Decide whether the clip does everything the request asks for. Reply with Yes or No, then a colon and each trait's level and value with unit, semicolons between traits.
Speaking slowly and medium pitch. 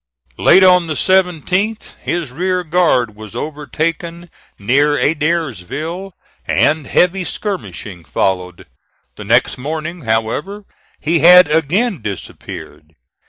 Yes: slow, 105 wpm; medium, 160 Hz